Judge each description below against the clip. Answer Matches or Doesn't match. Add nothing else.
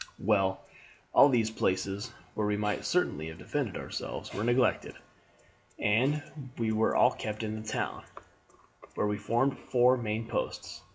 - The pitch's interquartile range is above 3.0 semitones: Doesn't match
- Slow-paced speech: Doesn't match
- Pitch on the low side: Matches